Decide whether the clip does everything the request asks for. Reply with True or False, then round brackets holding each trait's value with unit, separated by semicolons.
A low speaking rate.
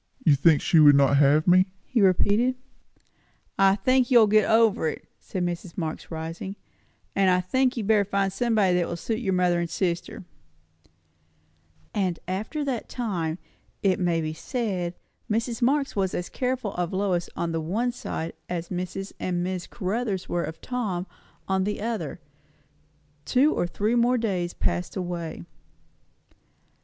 False (160 wpm)